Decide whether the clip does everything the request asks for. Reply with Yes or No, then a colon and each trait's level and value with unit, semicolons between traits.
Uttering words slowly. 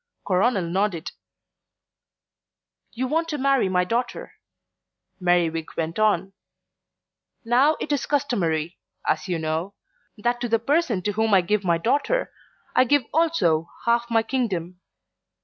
Yes: slow, 130 wpm